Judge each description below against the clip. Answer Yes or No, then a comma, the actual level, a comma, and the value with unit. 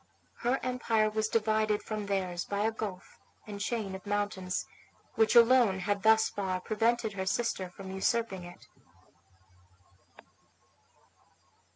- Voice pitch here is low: No, high, 210 Hz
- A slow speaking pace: Yes, slow, 120 wpm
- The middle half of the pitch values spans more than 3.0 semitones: No, average, 2.7 semitones